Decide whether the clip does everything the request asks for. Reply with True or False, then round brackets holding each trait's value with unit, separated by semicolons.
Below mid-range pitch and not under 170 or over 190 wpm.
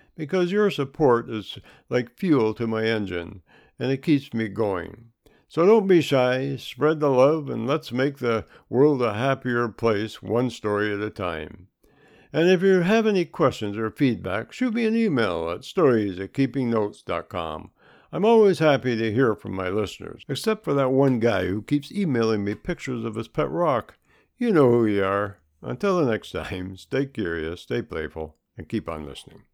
True (120 Hz; 180 wpm)